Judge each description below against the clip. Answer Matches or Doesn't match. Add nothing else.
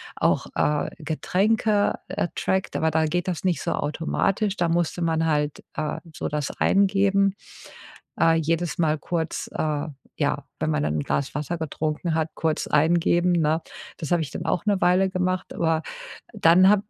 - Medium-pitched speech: Matches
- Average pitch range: Matches